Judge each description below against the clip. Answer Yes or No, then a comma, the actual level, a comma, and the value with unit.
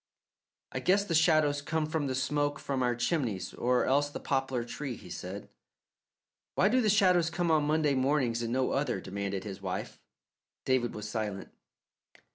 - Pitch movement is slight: No, average, 4.7 semitones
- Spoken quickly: No, average, 170 wpm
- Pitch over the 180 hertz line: No, low, 135 Hz